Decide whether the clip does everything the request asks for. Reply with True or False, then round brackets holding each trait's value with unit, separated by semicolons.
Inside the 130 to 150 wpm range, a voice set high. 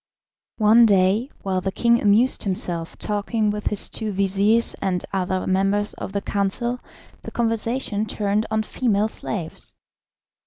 True (140 wpm; 205 Hz)